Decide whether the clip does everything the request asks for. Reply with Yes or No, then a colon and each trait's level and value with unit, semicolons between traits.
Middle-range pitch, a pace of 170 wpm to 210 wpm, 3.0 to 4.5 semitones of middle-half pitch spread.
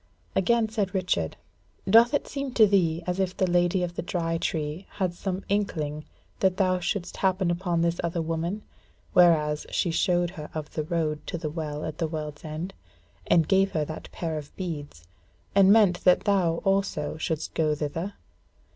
Yes: medium, 175 Hz; average, 180 wpm; average, 3.4 semitones